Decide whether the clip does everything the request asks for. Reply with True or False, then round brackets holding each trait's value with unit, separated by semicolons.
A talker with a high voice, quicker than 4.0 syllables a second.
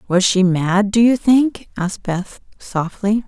False (200 Hz; 3.9 syllables/s)